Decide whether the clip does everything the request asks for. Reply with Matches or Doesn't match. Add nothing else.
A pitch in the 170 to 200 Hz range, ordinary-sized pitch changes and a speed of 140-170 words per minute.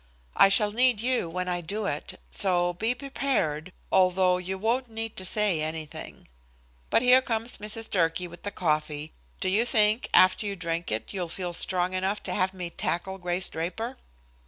Doesn't match